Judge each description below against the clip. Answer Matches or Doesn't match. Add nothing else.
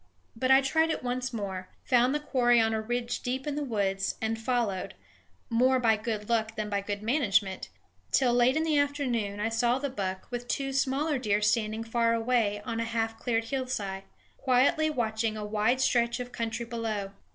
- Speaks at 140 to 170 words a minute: Doesn't match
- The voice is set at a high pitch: Matches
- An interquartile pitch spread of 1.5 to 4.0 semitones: Matches